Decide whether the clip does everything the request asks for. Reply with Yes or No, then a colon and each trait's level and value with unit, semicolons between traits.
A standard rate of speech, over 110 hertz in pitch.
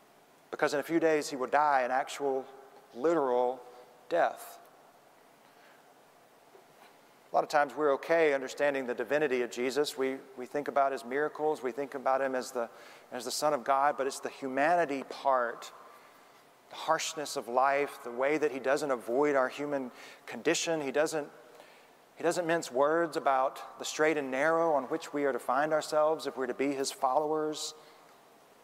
Yes: average, 170 wpm; medium, 140 Hz